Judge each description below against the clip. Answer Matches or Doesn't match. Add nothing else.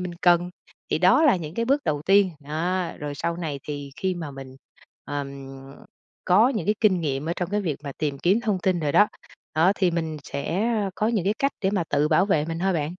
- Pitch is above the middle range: Doesn't match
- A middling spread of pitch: Matches